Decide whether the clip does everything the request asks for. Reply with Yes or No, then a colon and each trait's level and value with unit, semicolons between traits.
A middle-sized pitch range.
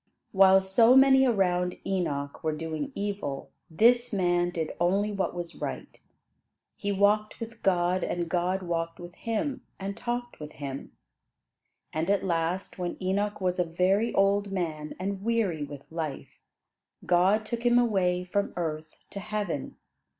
Yes: average, 3.3 semitones